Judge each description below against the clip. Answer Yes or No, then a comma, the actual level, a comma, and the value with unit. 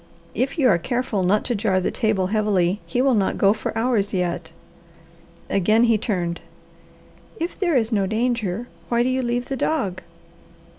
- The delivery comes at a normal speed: Yes, average, 170 wpm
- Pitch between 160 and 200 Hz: No, high, 220 Hz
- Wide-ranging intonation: No, average, 4.3 semitones